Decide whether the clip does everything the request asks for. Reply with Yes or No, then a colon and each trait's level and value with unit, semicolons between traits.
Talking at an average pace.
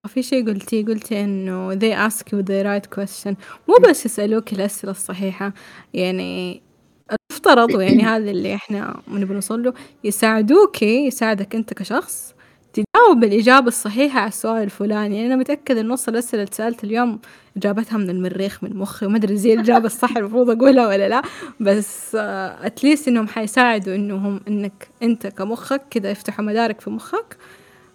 No: fast, 150 wpm